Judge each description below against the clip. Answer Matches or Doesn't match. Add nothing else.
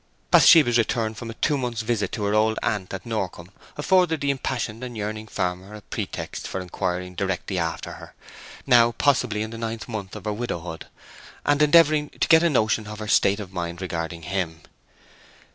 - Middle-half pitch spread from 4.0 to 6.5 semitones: Matches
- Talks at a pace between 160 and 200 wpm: Matches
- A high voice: Doesn't match